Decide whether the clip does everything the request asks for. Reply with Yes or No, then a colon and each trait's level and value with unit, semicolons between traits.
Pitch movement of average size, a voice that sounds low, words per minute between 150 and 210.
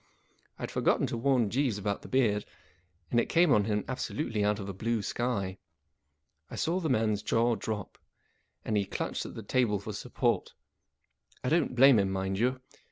Yes: average, 3.8 semitones; low, 110 Hz; average, 190 wpm